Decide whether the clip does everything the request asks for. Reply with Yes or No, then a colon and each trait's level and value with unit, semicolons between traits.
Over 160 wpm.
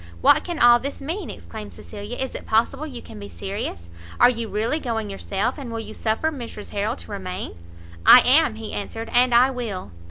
Yes: average, 200 wpm